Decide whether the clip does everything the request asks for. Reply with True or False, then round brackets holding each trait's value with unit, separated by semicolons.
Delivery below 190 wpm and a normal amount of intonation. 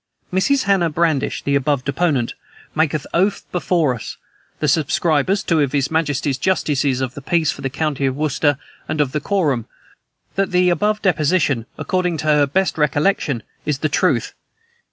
True (165 wpm; 4.2 semitones)